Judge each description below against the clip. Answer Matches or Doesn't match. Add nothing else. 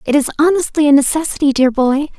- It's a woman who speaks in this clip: Matches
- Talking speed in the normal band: Matches